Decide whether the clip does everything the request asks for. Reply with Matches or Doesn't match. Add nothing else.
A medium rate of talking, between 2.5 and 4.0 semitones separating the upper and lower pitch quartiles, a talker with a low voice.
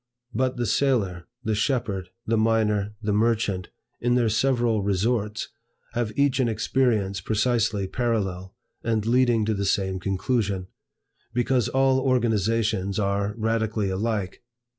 Doesn't match